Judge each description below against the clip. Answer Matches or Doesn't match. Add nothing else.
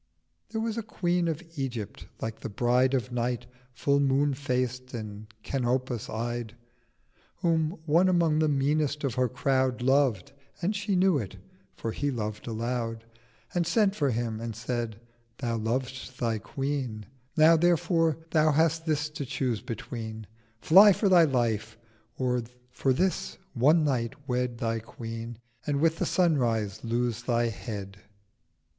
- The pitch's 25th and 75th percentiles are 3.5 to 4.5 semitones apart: Doesn't match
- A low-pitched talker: Matches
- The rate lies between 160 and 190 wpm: Doesn't match